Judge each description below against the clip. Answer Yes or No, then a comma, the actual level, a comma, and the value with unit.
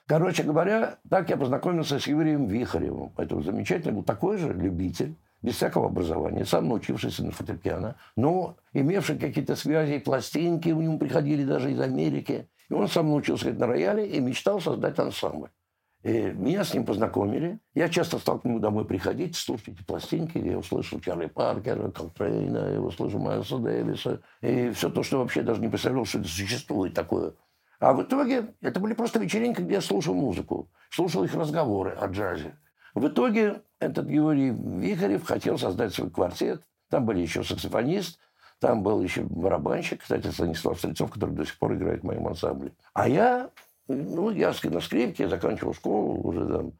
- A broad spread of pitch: Yes, wide, 6.9 semitones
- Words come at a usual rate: No, fast, 175 wpm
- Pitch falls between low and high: Yes, medium, 150 Hz